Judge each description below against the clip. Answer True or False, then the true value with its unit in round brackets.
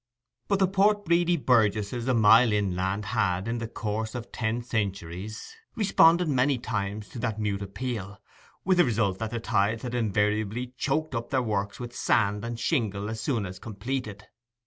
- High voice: False (115 Hz)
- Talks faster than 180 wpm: False (170 wpm)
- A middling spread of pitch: True (3.6 semitones)